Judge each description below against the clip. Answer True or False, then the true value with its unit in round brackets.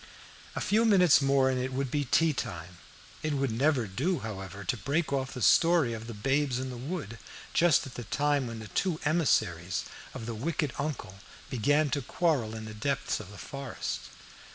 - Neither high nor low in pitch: False (130 Hz)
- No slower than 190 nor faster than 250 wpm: True (195 wpm)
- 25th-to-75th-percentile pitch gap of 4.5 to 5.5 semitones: True (5.0 semitones)